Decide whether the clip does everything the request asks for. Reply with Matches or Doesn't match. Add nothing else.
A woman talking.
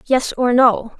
Matches